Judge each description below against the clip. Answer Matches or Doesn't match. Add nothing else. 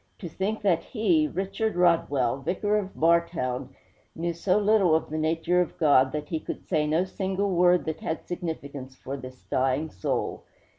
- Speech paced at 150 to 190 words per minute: Matches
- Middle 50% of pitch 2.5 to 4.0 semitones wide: Doesn't match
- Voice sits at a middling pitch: Matches